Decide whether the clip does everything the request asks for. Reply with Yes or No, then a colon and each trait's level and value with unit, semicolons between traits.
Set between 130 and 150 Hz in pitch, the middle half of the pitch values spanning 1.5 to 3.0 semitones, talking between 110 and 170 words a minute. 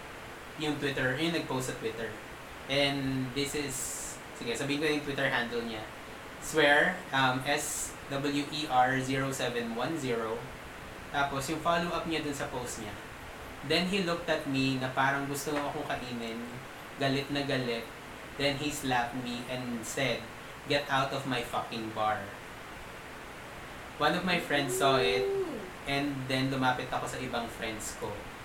Yes: low, 135 Hz; average, 2.7 semitones; average, 140 wpm